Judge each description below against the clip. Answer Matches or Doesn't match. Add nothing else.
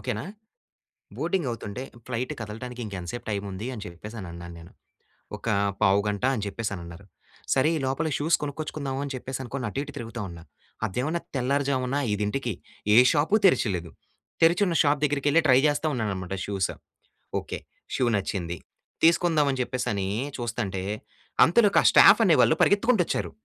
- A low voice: Matches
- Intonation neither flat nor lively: Doesn't match